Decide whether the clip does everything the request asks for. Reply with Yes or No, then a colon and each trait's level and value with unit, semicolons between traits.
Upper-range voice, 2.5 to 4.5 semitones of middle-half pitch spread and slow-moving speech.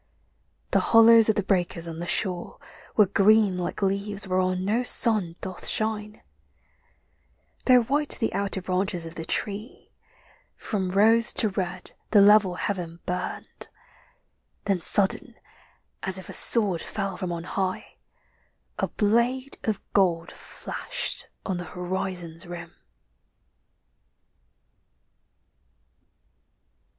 Yes: high, 195 Hz; average, 3.0 semitones; slow, 115 wpm